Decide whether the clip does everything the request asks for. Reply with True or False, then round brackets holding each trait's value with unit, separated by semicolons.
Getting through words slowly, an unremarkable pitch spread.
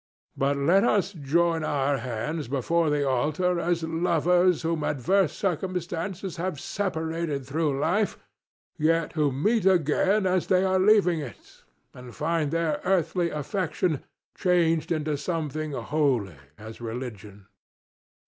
True (125 wpm; 4.0 semitones)